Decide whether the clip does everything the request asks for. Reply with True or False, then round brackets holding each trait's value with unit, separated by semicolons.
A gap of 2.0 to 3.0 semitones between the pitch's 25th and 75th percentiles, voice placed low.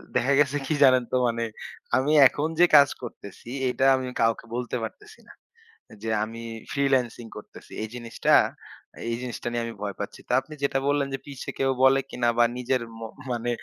True (2.7 semitones; 125 Hz)